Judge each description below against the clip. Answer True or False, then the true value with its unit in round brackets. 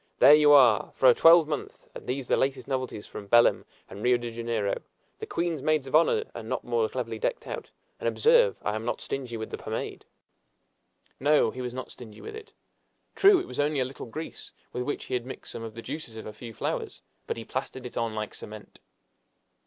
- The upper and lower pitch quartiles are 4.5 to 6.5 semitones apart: True (4.8 semitones)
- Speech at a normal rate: False (220 wpm)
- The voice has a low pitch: True (130 Hz)